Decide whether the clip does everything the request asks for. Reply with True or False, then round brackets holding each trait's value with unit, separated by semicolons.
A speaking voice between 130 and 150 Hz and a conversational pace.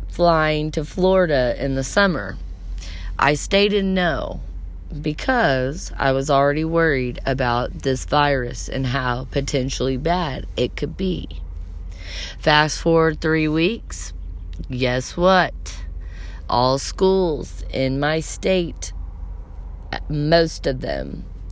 False (135 Hz; 105 wpm)